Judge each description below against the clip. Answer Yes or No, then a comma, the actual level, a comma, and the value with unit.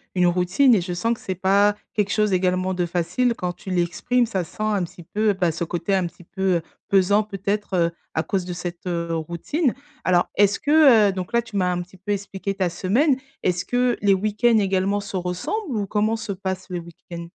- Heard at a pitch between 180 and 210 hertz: Yes, high, 190 Hz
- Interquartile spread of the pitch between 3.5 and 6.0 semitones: No, average, 2.9 semitones